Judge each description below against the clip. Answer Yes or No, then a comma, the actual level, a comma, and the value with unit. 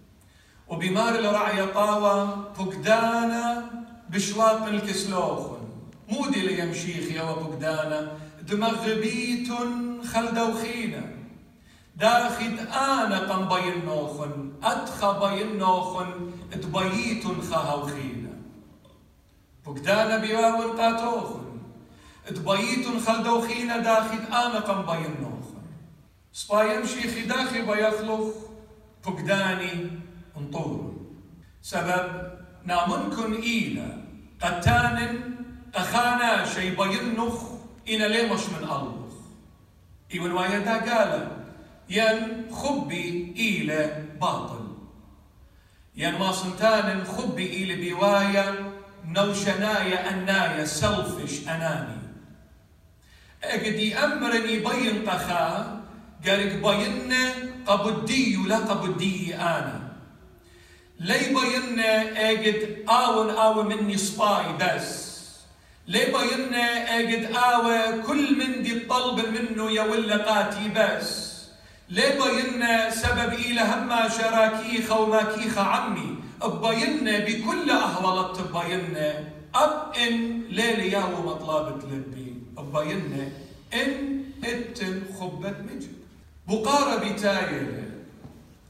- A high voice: Yes, high, 210 Hz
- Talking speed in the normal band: No, slow, 80 wpm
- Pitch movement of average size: Yes, average, 4.8 semitones